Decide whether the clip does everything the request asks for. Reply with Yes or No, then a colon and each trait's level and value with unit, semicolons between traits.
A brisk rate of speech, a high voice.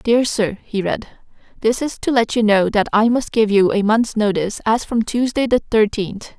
Yes: fast, 215 wpm; high, 220 Hz